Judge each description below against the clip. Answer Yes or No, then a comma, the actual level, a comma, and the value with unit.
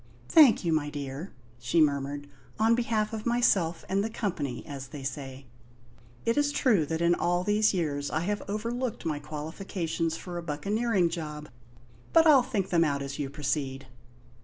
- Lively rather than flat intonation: Yes, wide, 6.5 semitones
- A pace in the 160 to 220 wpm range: Yes, average, 170 wpm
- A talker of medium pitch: Yes, medium, 165 Hz